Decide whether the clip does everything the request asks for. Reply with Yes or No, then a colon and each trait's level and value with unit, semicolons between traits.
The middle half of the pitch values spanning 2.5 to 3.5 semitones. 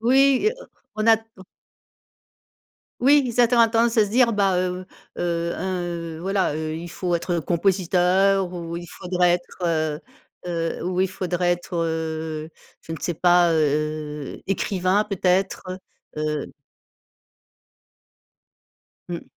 Yes: average, 2.9 semitones